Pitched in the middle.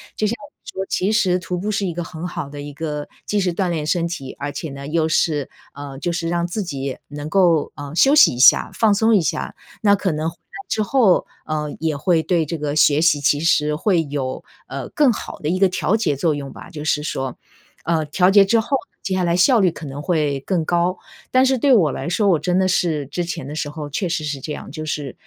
Yes: medium, 165 Hz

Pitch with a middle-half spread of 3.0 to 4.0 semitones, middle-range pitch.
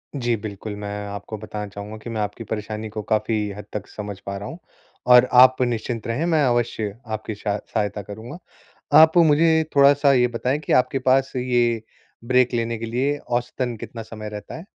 No: average, 3.3 semitones; low, 115 Hz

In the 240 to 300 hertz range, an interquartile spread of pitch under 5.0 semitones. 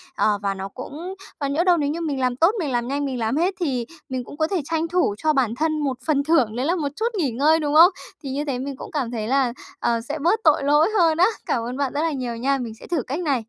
Yes: very high, 285 Hz; average, 4.2 semitones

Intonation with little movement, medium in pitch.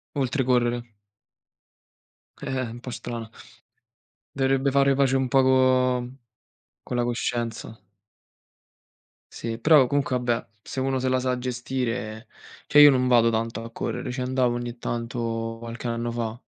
No: narrow, 1.9 semitones; low, 125 Hz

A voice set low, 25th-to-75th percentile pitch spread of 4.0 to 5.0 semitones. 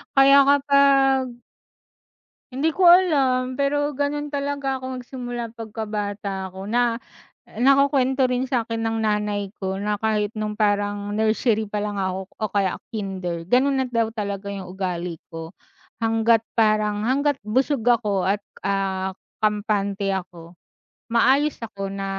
No: high, 220 Hz; average, 4.6 semitones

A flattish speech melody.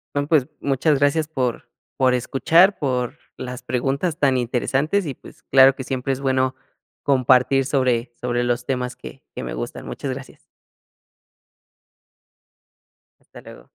Yes: narrow, 2.0 semitones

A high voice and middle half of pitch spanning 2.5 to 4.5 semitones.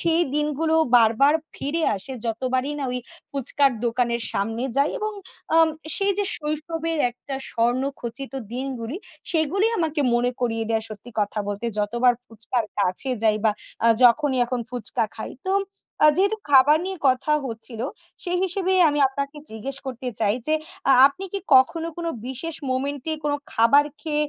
No: very high, 265 Hz; average, 4.9 semitones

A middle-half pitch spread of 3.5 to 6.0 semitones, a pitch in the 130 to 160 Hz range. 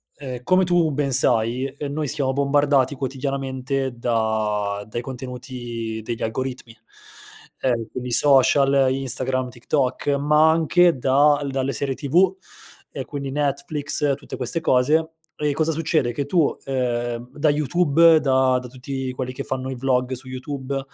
No: narrow, 2.5 semitones; low, 135 Hz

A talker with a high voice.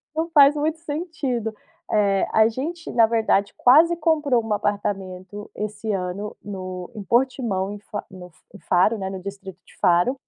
Yes: high, 210 Hz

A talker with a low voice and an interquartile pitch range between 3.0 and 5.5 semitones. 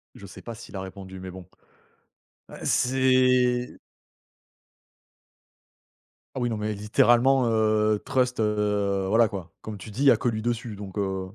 Yes: low, 110 Hz; average, 3.6 semitones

